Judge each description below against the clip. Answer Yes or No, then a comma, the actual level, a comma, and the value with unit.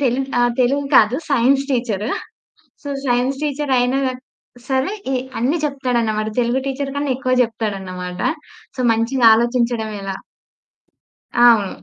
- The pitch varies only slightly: No, average, 3.3 semitones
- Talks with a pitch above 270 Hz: No, high, 245 Hz